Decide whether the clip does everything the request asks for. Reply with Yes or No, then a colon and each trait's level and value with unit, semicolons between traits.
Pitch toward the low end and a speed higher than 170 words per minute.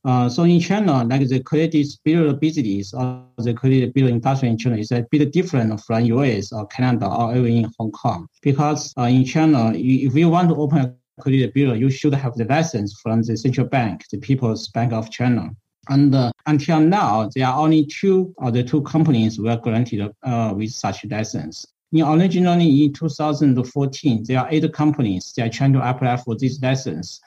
Yes: low, 130 Hz; fast, 205 wpm